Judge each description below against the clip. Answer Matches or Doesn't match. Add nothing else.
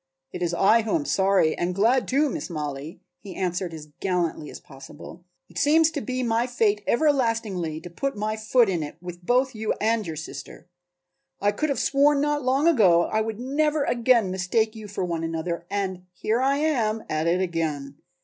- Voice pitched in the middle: Doesn't match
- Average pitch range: Doesn't match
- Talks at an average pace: Matches